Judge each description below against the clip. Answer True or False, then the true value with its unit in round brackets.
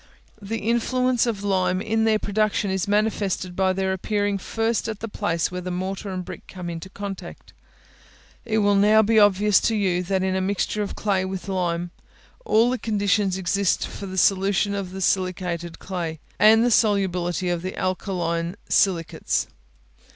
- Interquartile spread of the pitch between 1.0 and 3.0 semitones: True (2.4 semitones)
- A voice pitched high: True (195 Hz)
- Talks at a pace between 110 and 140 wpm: False (170 wpm)